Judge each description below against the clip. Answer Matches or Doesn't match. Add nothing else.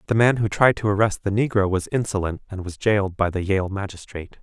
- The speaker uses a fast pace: Matches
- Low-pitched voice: Matches